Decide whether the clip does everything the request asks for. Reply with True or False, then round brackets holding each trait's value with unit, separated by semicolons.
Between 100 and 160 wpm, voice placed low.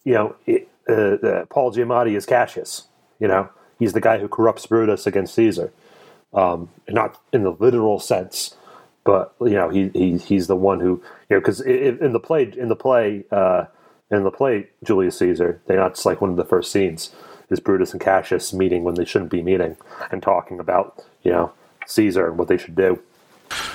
False (200 wpm; 115 Hz)